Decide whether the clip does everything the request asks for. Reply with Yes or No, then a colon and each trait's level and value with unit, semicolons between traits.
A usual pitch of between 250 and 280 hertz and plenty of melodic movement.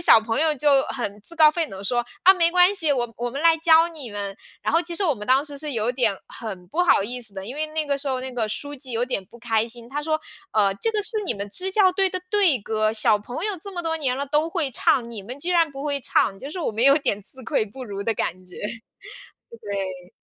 Yes: very high, 265 Hz; wide, 6.6 semitones